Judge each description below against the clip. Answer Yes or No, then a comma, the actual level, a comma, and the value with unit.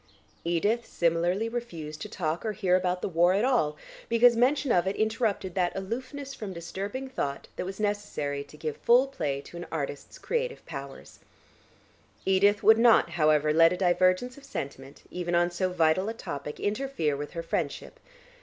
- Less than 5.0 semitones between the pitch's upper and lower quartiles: No, wide, 5.6 semitones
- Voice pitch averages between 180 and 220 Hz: Yes, medium, 185 Hz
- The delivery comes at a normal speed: Yes, average, 175 wpm